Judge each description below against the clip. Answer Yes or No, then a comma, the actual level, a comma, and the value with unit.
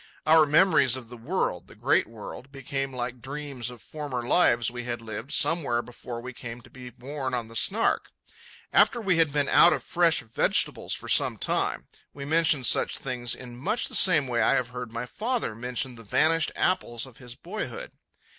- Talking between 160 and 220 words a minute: Yes, average, 195 wpm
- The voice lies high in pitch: No, low, 130 Hz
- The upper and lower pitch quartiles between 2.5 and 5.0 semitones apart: Yes, average, 4.5 semitones